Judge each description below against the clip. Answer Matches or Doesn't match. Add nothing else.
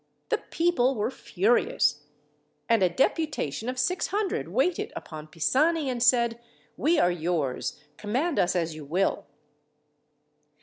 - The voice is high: Matches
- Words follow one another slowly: Matches